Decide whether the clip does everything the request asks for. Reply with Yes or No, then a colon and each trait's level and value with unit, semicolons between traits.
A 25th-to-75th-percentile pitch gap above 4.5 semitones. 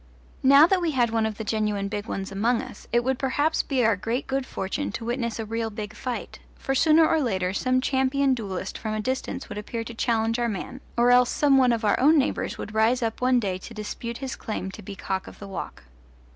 No: average, 3.6 semitones